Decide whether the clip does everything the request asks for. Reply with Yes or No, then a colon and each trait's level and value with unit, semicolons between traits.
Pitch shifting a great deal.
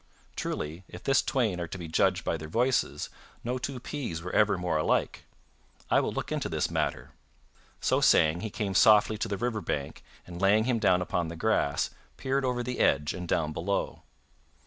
Yes: wide, 5.8 semitones